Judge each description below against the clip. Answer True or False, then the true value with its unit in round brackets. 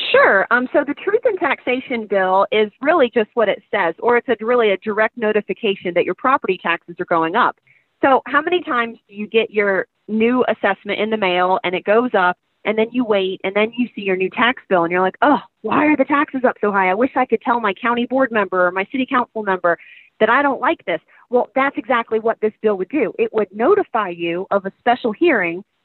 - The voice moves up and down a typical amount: True (4.4 semitones)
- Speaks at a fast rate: True (240 wpm)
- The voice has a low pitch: False (220 Hz)